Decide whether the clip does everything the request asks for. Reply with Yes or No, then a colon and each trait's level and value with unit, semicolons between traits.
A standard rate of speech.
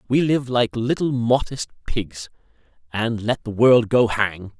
Yes: average, 155 wpm